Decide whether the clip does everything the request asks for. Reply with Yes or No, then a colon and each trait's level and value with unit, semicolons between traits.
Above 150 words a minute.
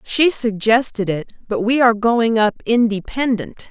No: average, 145 wpm